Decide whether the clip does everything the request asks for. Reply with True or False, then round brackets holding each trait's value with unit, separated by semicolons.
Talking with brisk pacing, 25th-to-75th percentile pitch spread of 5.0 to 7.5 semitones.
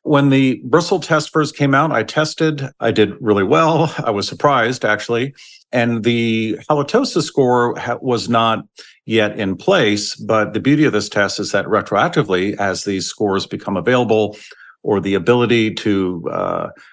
False (160 wpm; 5.4 semitones)